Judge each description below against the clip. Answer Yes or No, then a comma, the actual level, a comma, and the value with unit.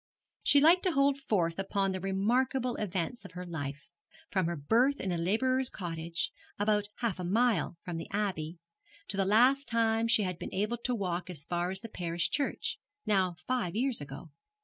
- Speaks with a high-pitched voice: Yes, high, 195 Hz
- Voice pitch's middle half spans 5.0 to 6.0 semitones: Yes, wide, 5.5 semitones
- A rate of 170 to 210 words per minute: Yes, average, 190 wpm